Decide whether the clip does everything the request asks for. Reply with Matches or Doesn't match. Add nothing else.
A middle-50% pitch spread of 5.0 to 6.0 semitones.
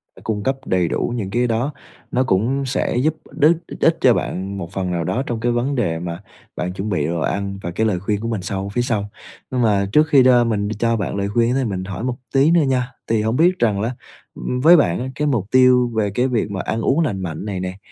Doesn't match